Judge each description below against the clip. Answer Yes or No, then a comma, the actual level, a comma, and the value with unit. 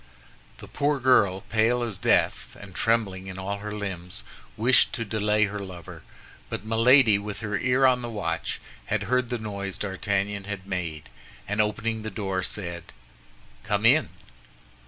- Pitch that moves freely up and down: No, average, 2.9 semitones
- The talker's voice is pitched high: No, low, 105 Hz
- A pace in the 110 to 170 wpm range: Yes, average, 155 wpm